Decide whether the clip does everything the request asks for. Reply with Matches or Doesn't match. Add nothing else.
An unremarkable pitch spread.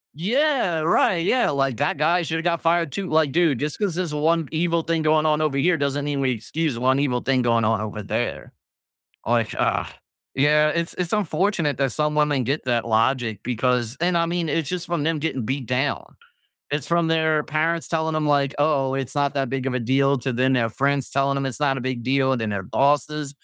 Matches